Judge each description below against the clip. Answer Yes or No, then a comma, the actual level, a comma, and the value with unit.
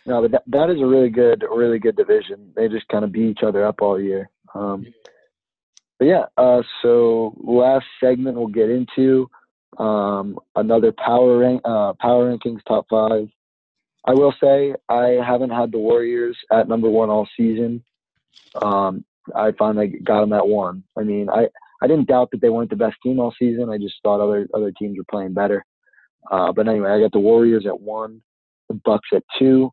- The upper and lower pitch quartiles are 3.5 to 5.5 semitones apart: No, average, 2.9 semitones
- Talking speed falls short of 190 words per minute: No, average, 195 wpm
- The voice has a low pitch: Yes, low, 115 Hz